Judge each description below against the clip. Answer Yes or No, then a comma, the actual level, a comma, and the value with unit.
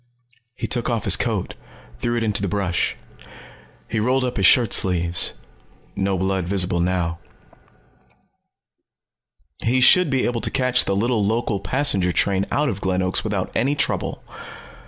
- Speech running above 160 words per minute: No, average, 155 wpm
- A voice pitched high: No, low, 100 Hz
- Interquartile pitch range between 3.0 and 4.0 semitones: No, average, 4.7 semitones